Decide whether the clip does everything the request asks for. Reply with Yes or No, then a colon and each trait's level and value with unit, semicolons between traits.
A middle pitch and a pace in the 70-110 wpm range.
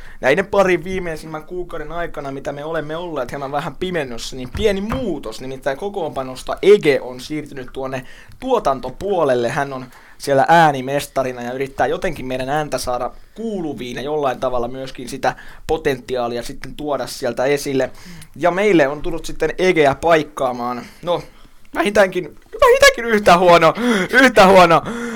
No: medium, 150 Hz; average, 135 wpm